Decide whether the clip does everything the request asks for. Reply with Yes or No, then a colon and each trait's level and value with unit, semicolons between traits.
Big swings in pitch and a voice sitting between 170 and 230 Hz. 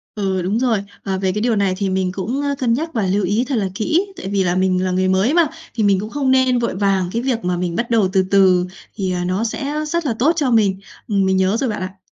No: average, 4.4 semitones; high, 200 Hz